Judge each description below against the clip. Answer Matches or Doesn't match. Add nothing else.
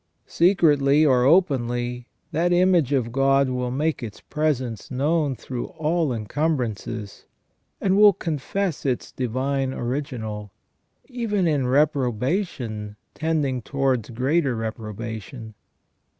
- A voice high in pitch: Doesn't match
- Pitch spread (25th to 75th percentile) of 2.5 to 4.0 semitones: Doesn't match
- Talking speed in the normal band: Doesn't match